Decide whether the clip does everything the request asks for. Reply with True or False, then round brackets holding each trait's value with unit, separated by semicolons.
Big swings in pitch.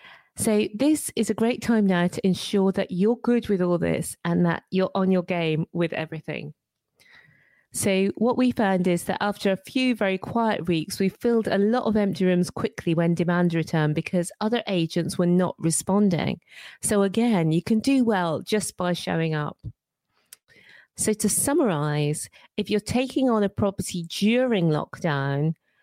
False (4.2 semitones)